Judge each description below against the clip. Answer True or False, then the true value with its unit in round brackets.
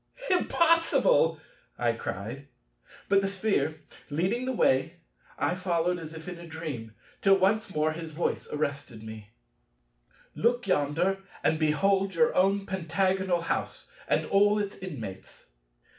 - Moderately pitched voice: True (175 Hz)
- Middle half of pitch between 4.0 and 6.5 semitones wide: True (4.7 semitones)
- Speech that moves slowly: True (130 wpm)